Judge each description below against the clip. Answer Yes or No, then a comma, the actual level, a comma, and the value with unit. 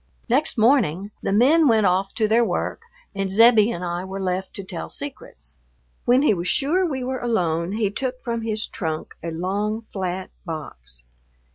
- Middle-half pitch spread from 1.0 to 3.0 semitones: No, average, 4.8 semitones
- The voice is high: Yes, high, 205 Hz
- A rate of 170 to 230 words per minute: Yes, average, 175 wpm